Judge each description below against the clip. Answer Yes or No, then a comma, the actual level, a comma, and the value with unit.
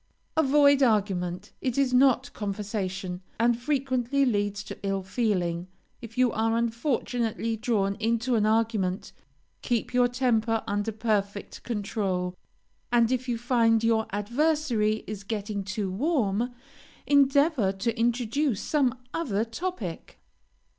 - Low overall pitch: No, high, 225 Hz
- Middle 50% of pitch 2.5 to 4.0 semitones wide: Yes, average, 3.5 semitones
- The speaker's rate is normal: No, slow, 120 wpm